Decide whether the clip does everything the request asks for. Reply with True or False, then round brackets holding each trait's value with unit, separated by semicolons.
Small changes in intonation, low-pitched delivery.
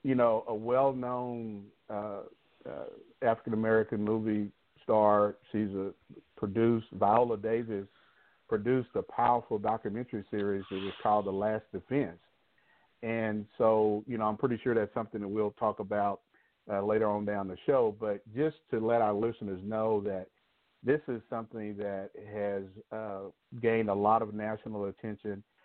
True (1.8 semitones; 110 Hz)